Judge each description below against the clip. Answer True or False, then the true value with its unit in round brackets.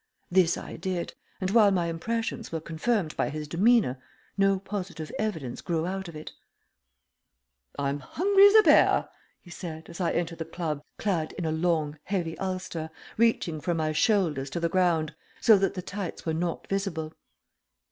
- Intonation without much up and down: False (3.7 semitones)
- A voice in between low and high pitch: True (175 Hz)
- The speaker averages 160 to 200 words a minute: True (170 wpm)